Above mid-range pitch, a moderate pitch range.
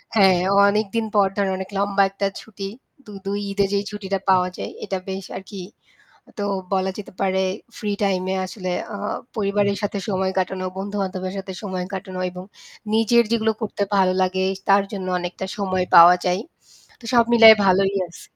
No: high, 195 Hz; narrow, 1.5 semitones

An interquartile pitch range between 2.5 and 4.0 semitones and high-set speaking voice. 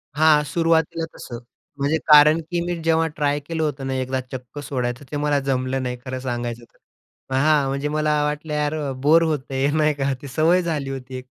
No: average, 2.8 semitones; medium, 145 Hz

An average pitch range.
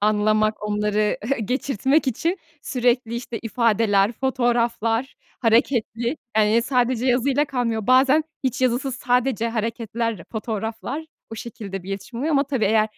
Yes: average, 3.0 semitones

